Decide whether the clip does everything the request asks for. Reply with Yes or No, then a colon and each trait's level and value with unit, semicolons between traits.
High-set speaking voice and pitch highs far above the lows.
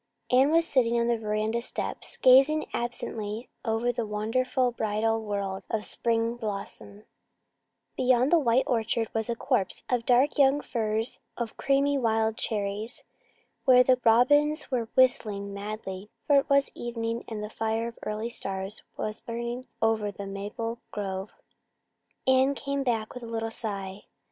No: high, 230 Hz; average, 3.0 semitones